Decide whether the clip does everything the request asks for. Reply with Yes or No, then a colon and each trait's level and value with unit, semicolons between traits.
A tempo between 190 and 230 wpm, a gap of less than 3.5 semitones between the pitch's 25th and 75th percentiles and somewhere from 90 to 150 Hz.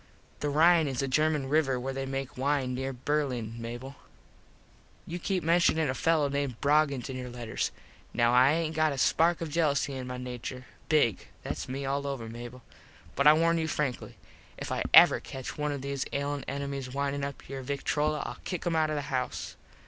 Yes: average, 195 wpm; average, 2.9 semitones; medium, 140 Hz